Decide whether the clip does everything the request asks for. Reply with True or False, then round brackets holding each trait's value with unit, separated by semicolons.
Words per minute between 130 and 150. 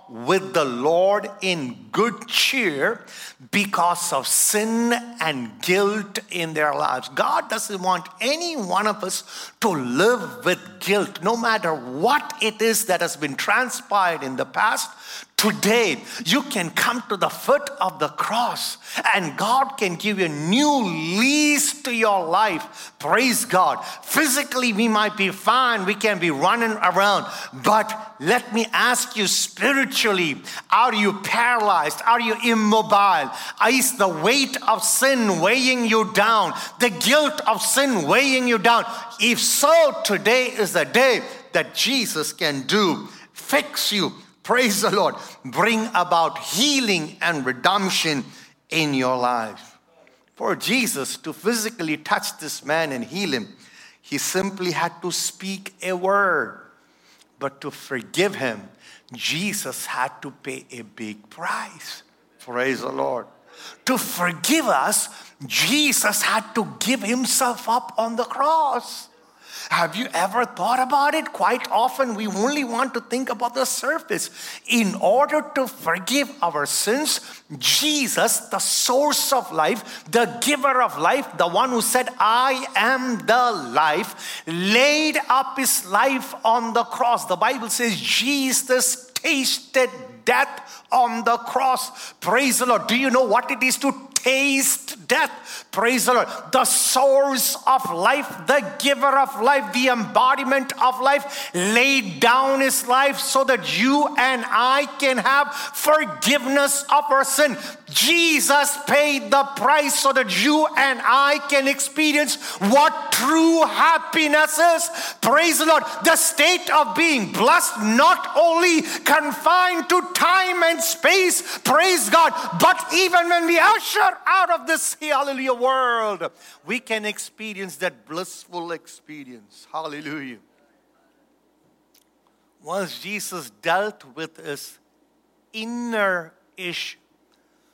True (140 wpm)